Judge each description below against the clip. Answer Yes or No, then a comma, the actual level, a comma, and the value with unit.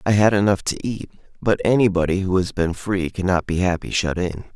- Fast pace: Yes, fast, 210 wpm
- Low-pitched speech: Yes, very low, 95 Hz